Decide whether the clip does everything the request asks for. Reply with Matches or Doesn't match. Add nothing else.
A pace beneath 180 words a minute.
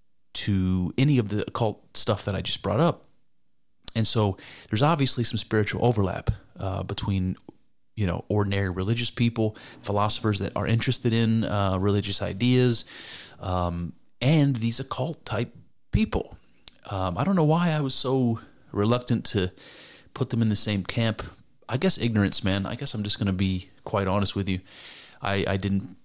Matches